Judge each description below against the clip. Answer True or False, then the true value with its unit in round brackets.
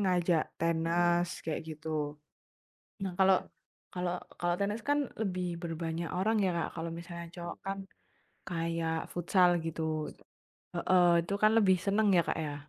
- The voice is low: False (175 Hz)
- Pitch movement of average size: False (2.2 semitones)